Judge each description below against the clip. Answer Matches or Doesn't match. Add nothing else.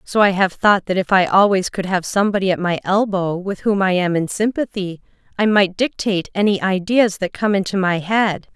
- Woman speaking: Matches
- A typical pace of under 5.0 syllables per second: Doesn't match